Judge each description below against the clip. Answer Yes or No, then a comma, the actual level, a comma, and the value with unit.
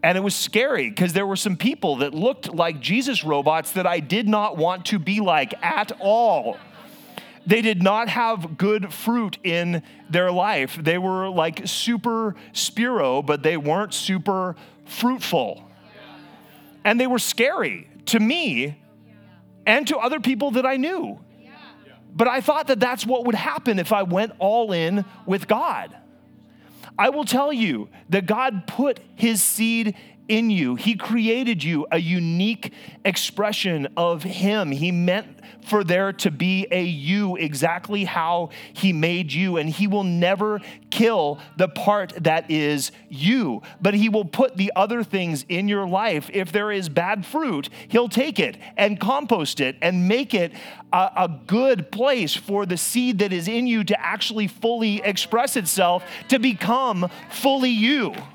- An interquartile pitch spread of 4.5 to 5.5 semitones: Yes, average, 4.8 semitones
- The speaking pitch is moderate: No, high, 200 Hz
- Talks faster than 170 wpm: No, average, 160 wpm